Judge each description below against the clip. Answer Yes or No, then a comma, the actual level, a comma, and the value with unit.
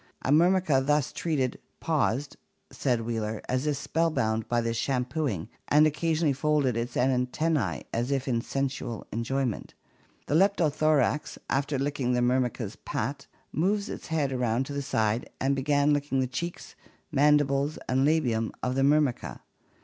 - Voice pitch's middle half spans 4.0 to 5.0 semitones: No, average, 3.3 semitones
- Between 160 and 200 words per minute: No, average, 150 wpm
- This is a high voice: No, low, 135 Hz